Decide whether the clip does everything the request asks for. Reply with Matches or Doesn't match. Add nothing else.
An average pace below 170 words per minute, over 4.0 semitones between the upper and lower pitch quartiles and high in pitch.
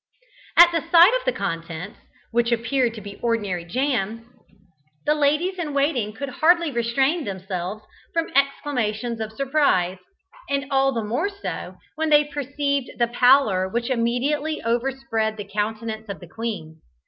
Matches